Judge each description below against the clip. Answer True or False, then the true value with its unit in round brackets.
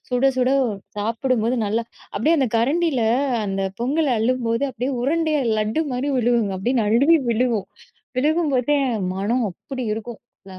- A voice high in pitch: True (250 Hz)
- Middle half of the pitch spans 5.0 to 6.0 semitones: False (3.8 semitones)